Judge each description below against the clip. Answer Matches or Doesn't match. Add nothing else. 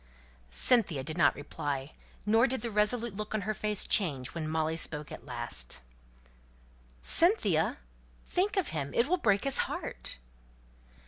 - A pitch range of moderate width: Doesn't match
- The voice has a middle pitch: Doesn't match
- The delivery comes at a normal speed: Matches